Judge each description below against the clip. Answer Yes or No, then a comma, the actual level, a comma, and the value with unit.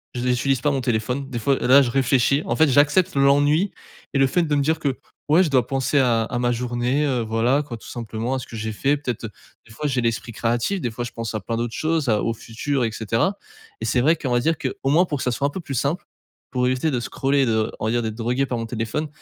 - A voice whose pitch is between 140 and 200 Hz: No, low, 130 Hz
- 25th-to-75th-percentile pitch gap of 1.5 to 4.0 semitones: Yes, average, 3.5 semitones